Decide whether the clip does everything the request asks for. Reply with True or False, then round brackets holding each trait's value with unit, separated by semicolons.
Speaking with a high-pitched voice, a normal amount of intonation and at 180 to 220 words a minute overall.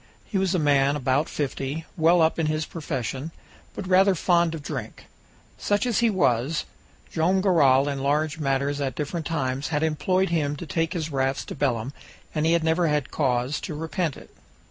False (155 Hz; 3.4 semitones; 190 wpm)